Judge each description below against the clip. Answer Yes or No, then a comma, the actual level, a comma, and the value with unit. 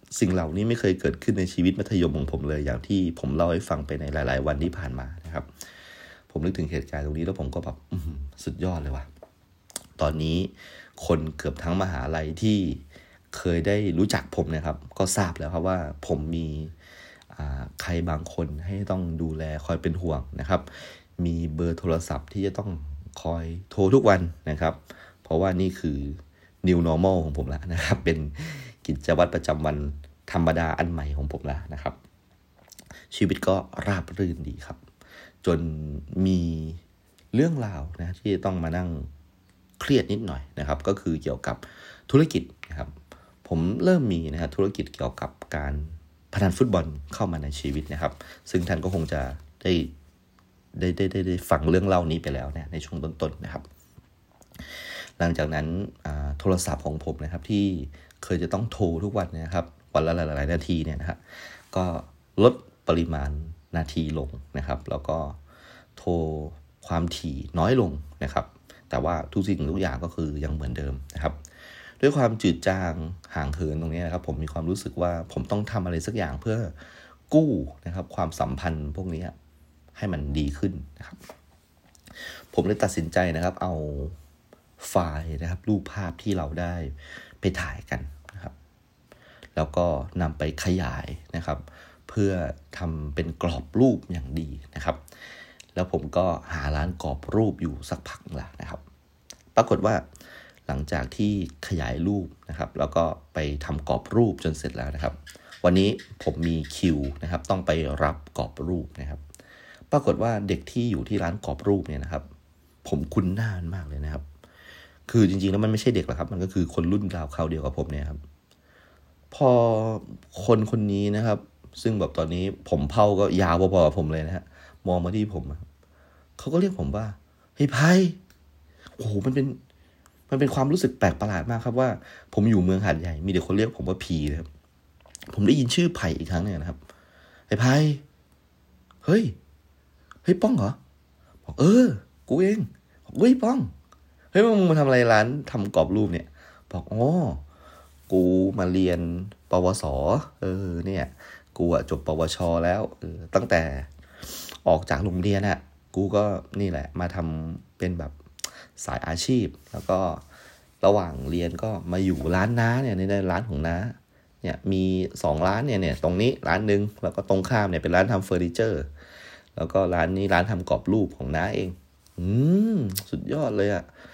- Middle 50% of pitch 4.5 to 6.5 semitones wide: No, average, 4.1 semitones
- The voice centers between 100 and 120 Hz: No, very low, 85 Hz